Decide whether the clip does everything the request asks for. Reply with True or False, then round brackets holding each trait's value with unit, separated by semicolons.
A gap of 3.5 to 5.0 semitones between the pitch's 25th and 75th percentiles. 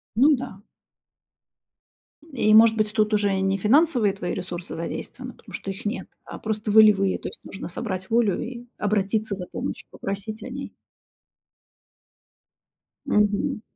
False (2.5 semitones)